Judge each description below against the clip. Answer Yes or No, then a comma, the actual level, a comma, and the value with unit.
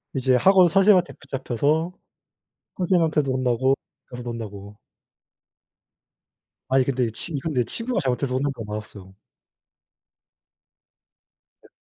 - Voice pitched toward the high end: No, low, 130 Hz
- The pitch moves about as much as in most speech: Yes, average, 5.0 semitones